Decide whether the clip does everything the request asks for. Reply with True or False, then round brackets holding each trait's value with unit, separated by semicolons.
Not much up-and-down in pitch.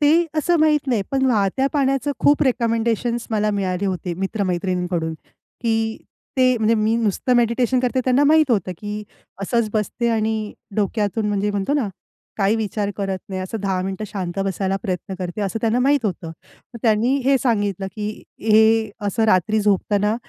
False (3.6 semitones)